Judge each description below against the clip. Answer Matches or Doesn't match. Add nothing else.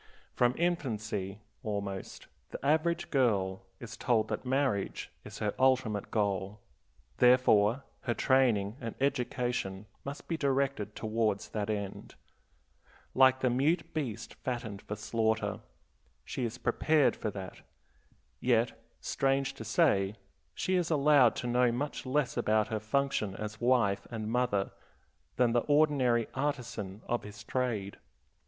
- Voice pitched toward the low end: Matches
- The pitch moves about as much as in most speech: Matches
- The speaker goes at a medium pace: Doesn't match